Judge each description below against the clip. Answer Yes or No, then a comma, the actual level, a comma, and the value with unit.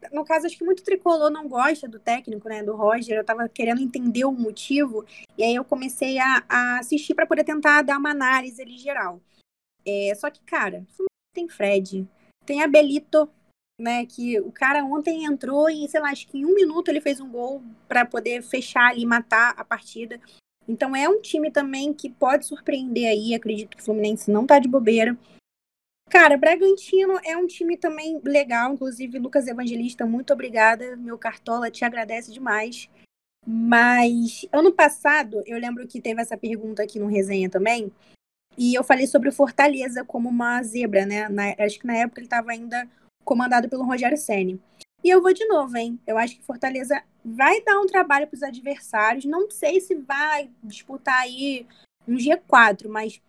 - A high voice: Yes, very high, 250 Hz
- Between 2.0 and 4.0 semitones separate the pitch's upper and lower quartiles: No, average, 4.4 semitones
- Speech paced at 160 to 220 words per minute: Yes, average, 180 wpm